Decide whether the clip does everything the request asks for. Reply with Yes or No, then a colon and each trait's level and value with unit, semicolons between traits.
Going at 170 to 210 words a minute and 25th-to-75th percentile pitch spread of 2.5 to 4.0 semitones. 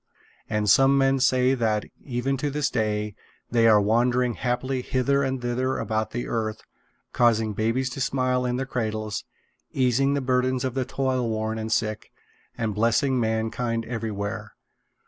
No: average, 150 wpm; average, 2.9 semitones